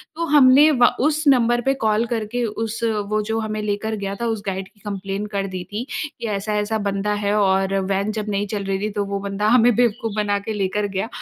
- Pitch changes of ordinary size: No, narrow, 2.2 semitones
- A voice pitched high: Yes, high, 210 Hz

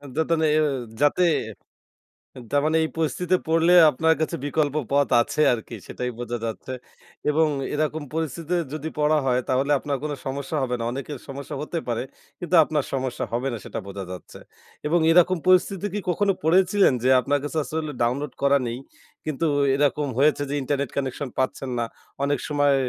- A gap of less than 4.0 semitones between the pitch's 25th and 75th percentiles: Yes, average, 3.3 semitones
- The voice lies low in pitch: No, medium, 145 Hz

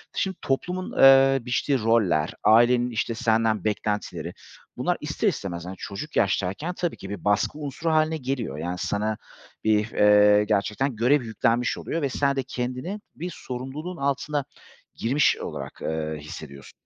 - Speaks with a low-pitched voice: Yes, low, 120 Hz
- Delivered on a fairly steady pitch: No, average, 5.1 semitones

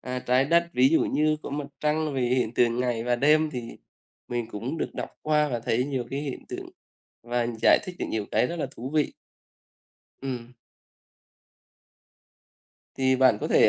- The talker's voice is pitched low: Yes, low, 130 Hz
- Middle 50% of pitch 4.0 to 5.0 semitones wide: No, average, 3.6 semitones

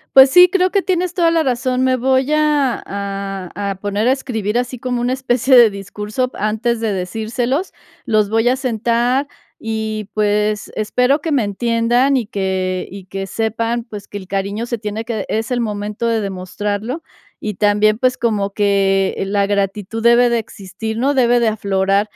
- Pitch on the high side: Yes, high, 220 Hz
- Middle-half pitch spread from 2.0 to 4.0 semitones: Yes, average, 3.6 semitones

